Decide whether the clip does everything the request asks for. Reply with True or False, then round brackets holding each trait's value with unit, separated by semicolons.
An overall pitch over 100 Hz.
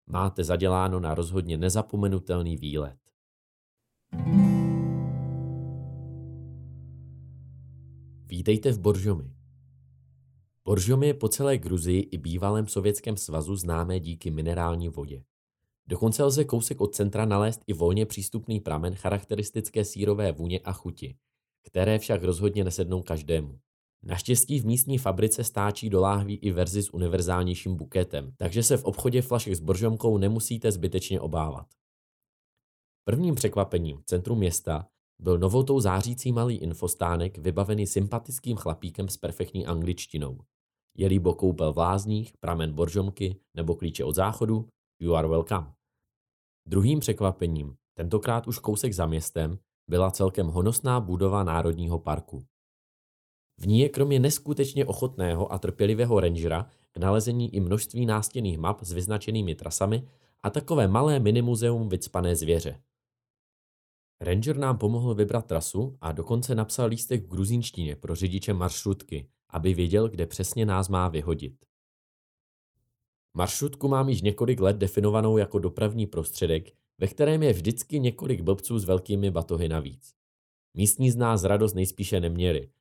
False (95 Hz)